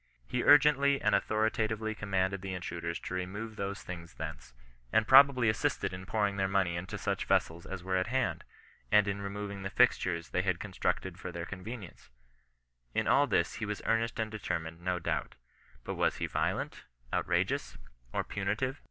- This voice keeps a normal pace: Yes, average, 175 wpm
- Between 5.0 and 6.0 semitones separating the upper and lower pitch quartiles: No, average, 3.3 semitones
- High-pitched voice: No, low, 100 Hz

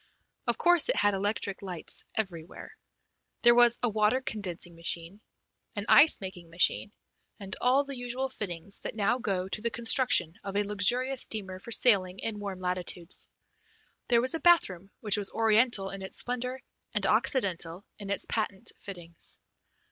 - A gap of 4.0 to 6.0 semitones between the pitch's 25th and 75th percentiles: Yes, average, 4.3 semitones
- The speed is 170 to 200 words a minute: No, average, 160 wpm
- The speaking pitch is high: Yes, high, 205 Hz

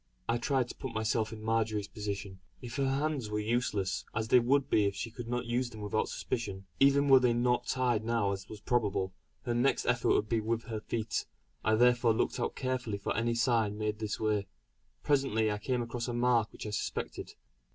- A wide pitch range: No, narrow, 2.5 semitones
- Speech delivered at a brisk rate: Yes, fast, 210 wpm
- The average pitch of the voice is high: No, low, 115 Hz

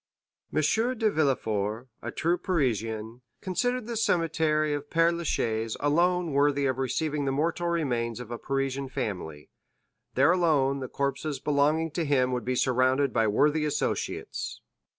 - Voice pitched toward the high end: No, medium, 140 Hz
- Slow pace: No, average, 145 wpm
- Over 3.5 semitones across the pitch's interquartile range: Yes, average, 4.3 semitones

